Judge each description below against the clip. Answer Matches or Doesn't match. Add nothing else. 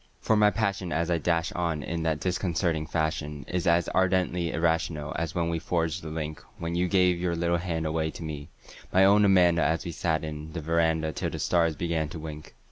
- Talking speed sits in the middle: Doesn't match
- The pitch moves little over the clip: Matches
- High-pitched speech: Doesn't match